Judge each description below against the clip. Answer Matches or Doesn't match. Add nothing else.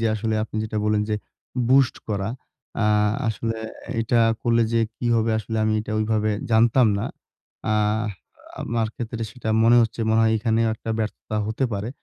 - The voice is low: Matches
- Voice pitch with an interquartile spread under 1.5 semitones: Matches